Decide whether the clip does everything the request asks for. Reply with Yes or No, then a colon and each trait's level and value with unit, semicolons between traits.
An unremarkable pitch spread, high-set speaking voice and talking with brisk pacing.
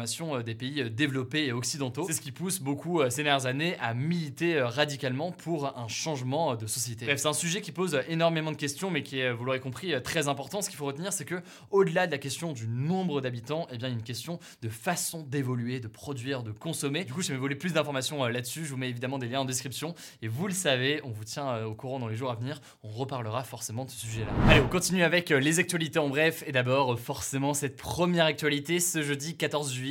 No: average, 4.2 semitones; medium, 140 Hz; fast, 265 wpm